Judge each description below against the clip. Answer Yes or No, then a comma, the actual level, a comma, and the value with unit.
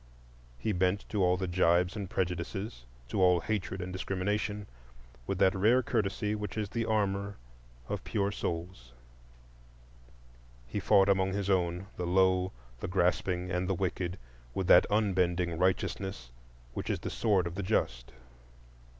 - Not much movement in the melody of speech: Yes, narrow, 2.1 semitones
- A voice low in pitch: Yes, very low, 95 Hz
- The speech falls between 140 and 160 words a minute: Yes, average, 150 wpm